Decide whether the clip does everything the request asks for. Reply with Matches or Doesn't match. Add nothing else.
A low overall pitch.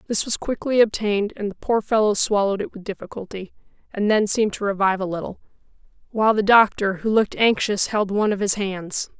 Doesn't match